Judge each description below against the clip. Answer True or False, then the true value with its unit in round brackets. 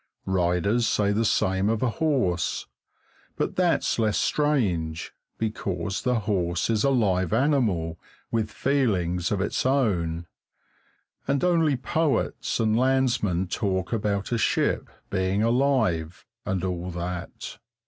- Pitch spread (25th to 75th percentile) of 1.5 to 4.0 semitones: False (5.5 semitones)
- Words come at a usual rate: False (125 wpm)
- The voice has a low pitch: True (105 Hz)